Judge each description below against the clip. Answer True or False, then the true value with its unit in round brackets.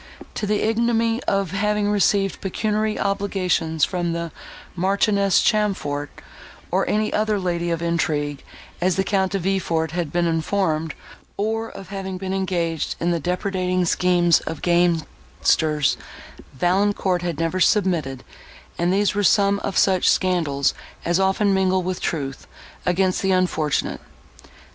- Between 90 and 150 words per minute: True (135 wpm)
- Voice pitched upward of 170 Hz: True (185 Hz)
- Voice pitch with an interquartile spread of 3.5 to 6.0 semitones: False (2.9 semitones)